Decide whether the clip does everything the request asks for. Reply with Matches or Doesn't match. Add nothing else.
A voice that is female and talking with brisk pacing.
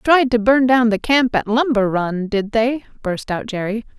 Matches